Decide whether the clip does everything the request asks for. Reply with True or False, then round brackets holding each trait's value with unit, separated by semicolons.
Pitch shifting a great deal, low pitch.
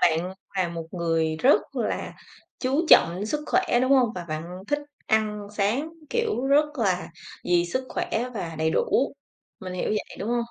False (6.9 semitones; 205 Hz)